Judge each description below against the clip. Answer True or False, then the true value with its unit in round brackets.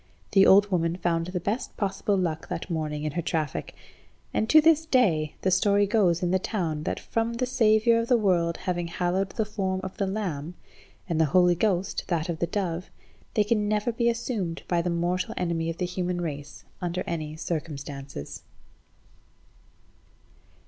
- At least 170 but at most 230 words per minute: True (175 wpm)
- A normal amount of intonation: True (3.8 semitones)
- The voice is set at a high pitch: False (180 Hz)